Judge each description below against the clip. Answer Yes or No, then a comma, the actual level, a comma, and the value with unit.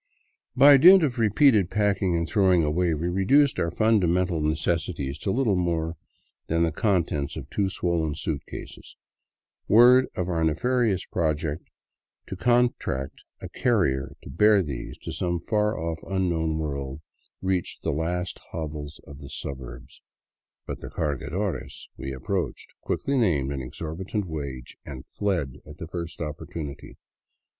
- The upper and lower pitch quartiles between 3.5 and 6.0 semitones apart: Yes, average, 4.8 semitones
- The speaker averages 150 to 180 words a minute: No, average, 140 wpm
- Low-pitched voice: Yes, very low, 85 Hz